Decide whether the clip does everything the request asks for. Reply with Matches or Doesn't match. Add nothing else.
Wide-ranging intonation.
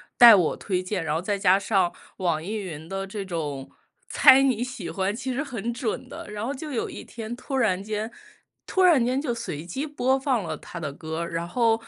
Matches